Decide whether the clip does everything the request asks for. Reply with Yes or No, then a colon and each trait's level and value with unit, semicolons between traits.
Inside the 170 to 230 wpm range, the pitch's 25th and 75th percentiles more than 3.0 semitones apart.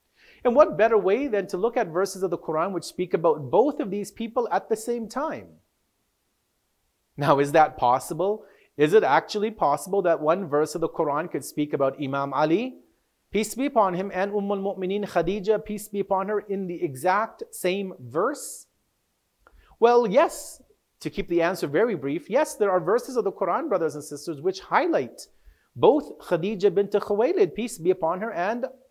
Yes: average, 185 wpm; average, 4.4 semitones